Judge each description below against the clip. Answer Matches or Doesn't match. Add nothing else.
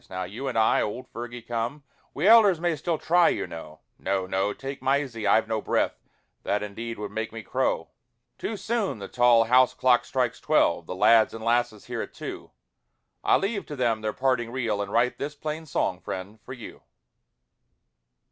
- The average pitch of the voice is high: Doesn't match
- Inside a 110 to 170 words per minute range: Doesn't match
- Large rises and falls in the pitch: Doesn't match